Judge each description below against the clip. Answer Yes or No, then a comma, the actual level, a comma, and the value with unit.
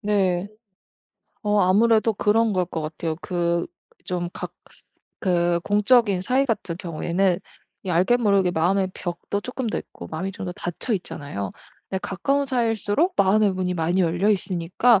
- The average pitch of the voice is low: No, high, 190 Hz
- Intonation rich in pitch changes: No, average, 3.4 semitones